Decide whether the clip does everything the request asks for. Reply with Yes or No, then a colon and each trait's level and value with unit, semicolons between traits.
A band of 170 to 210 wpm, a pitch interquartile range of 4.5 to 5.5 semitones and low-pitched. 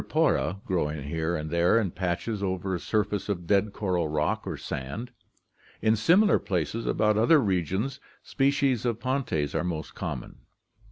No: average, 155 wpm; average, 5.0 semitones; low, 100 Hz